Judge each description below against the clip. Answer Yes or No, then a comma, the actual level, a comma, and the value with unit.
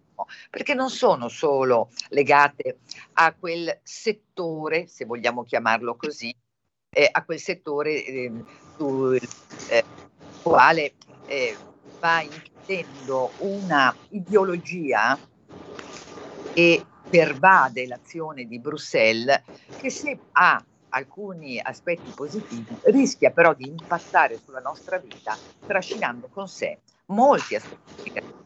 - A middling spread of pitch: No, wide, 6.2 semitones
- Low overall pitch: No, medium, 160 Hz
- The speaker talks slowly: Yes, slow, 105 wpm